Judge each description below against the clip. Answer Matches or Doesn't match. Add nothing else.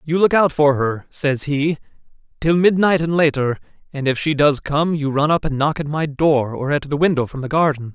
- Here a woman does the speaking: Doesn't match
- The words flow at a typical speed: Doesn't match